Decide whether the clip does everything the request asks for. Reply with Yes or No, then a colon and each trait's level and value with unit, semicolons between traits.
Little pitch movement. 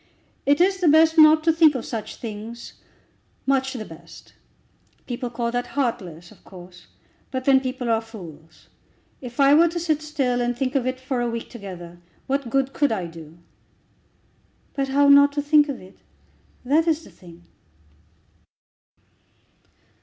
No: average, 4.5 semitones